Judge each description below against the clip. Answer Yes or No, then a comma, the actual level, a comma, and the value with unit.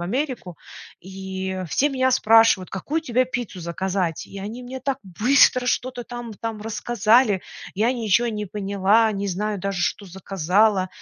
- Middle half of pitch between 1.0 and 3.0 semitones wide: No, average, 4.2 semitones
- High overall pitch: Yes, high, 210 Hz